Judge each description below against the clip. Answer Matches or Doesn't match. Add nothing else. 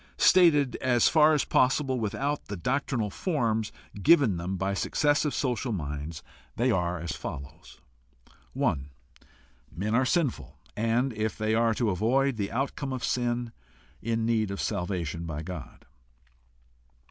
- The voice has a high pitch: Doesn't match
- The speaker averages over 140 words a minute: Doesn't match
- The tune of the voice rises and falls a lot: Matches